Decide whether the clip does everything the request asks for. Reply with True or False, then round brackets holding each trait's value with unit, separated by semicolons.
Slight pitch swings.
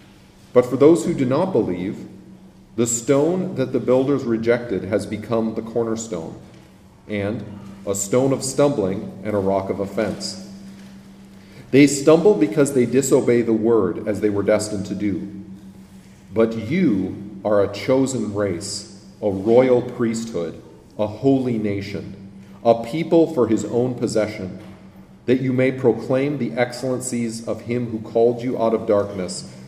False (4.3 semitones)